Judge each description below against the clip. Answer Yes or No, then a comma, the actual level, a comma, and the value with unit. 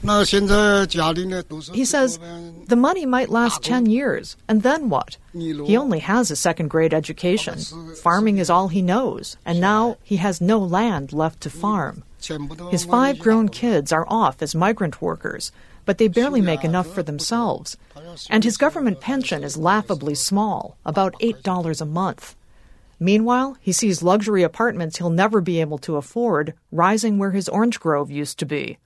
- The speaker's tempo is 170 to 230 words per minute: No, average, 160 wpm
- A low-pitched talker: No, high, 190 Hz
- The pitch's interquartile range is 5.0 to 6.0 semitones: Yes, average, 5.3 semitones